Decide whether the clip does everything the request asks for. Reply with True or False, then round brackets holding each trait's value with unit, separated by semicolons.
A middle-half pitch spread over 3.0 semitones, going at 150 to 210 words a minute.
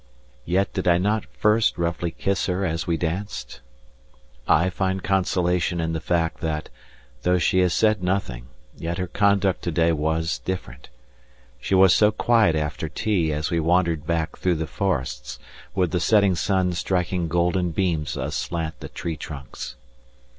False (2.6 semitones; 160 wpm)